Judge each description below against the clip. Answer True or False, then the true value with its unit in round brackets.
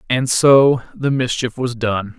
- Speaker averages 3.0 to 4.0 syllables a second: True (3.7 syllables/s)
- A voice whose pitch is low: True (125 Hz)